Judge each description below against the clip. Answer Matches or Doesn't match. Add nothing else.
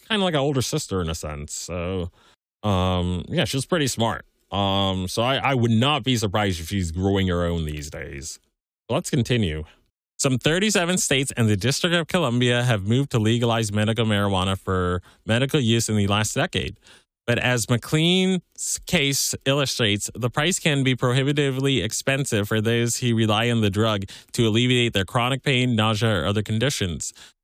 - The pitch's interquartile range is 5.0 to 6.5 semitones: Matches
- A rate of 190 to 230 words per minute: Doesn't match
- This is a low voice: Matches